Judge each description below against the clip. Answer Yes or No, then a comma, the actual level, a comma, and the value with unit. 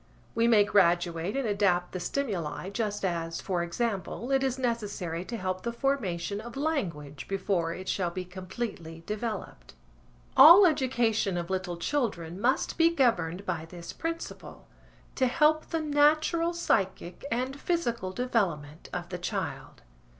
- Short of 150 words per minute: Yes, average, 140 wpm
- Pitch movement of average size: No, wide, 6.8 semitones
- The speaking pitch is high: Yes, high, 205 Hz